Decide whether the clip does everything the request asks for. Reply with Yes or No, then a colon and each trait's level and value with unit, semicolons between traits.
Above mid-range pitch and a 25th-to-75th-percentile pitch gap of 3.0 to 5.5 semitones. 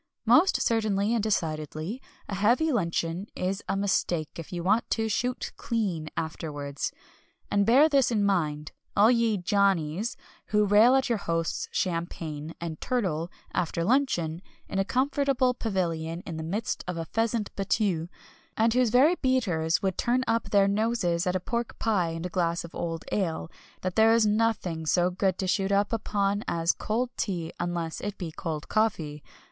Yes: high, 195 Hz; average, 5.2 semitones